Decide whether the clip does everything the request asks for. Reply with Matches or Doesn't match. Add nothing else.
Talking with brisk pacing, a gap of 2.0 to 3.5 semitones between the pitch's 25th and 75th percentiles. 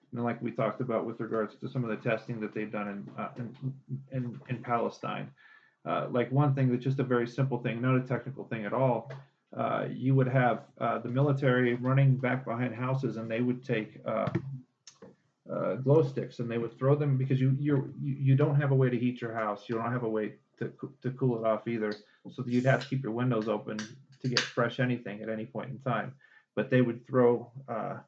Matches